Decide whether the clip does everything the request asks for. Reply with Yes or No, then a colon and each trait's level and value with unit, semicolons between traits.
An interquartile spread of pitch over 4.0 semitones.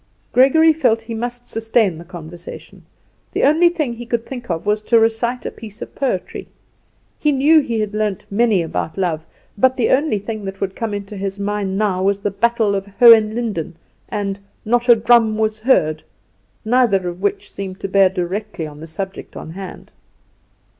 No: average, 3.7 semitones